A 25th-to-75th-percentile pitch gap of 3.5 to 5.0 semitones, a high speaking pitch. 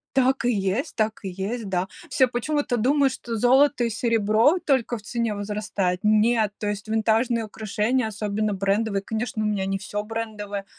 No: average, 2.8 semitones; high, 220 Hz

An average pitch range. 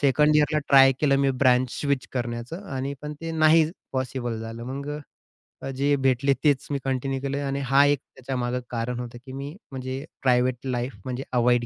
No: narrow, 2.1 semitones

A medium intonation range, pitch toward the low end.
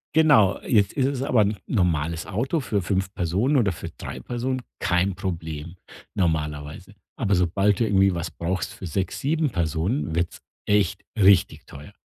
Yes: average, 4.5 semitones; very low, 95 Hz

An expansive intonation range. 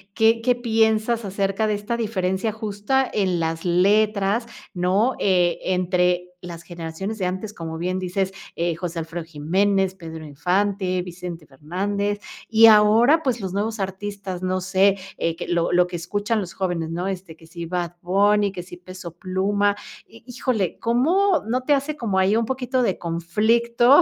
No: average, 3.7 semitones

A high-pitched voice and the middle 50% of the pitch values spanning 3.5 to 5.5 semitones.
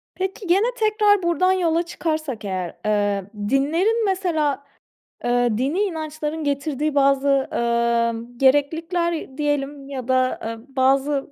Yes: very high, 285 Hz; average, 4.9 semitones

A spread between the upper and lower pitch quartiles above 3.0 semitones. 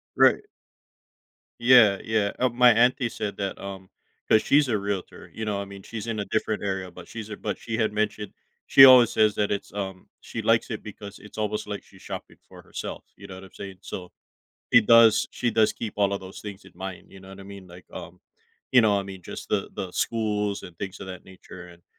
No: narrow, 2.4 semitones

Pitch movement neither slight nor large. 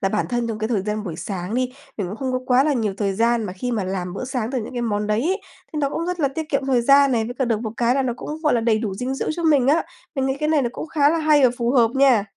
Yes: average, 4.3 semitones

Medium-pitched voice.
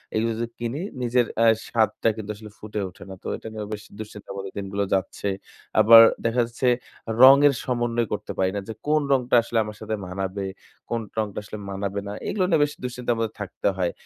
No: low, 110 Hz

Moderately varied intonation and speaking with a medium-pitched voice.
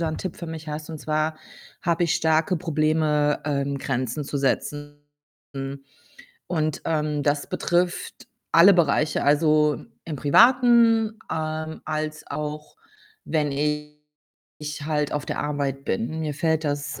No: narrow, 1.6 semitones; medium, 150 Hz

